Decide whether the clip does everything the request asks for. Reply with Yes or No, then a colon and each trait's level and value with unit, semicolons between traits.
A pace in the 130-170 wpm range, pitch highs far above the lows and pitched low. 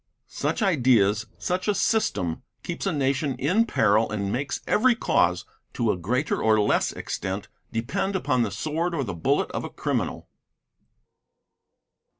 Yes: average, 150 wpm; wide, 8.9 semitones; low, 130 Hz